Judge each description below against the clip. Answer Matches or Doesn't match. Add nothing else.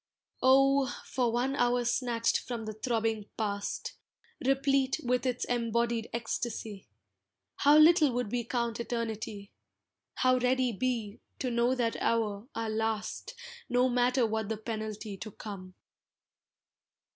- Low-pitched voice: Doesn't match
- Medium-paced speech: Doesn't match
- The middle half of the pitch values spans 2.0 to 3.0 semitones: Matches